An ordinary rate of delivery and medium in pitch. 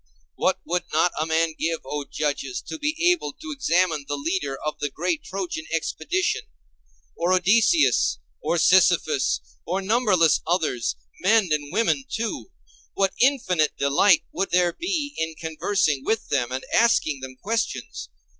Yes: average, 145 wpm; medium, 175 Hz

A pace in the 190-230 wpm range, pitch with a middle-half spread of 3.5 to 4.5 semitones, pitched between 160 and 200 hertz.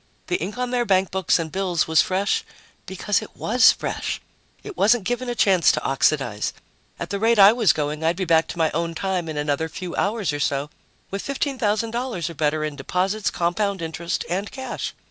No: average, 195 wpm; average, 5.1 semitones; medium, 185 Hz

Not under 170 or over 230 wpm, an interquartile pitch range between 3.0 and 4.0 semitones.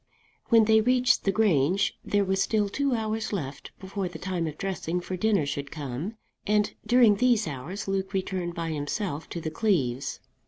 No: average, 180 wpm; average, 5.1 semitones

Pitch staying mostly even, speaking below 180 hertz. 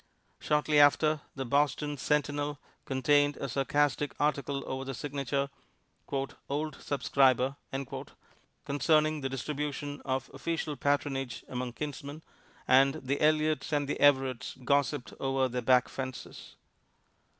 Yes: narrow, 1.7 semitones; medium, 140 Hz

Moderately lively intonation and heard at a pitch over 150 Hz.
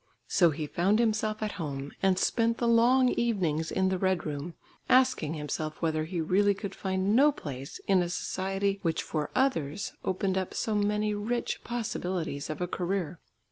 Yes: average, 4.7 semitones; high, 190 Hz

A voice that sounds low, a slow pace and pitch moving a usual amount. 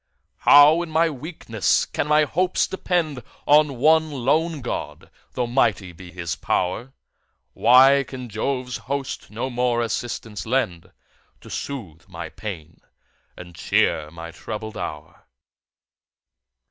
No: low, 125 Hz; slow, 120 wpm; wide, 6.8 semitones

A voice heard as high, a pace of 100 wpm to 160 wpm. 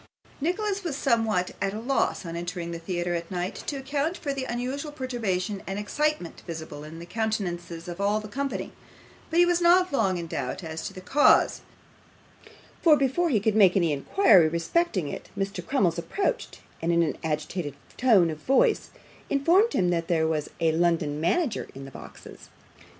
No: high, 195 Hz; average, 180 wpm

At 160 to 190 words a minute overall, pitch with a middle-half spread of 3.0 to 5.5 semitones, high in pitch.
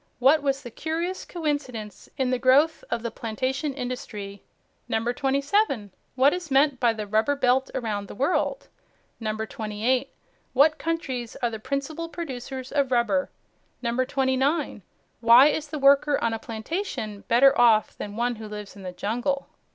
No: average, 150 wpm; average, 4.0 semitones; very high, 255 Hz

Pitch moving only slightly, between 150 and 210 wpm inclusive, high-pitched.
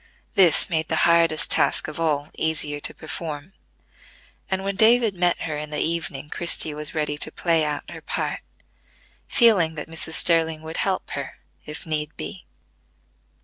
No: narrow, 2.3 semitones; average, 160 wpm; medium, 160 Hz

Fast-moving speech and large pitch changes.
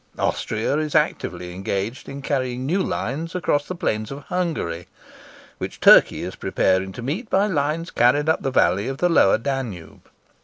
No: average, 165 wpm; wide, 6.9 semitones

